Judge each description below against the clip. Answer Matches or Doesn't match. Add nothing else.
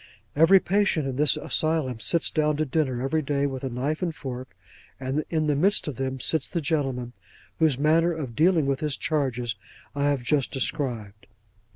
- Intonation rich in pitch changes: Doesn't match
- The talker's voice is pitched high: Doesn't match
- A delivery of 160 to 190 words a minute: Matches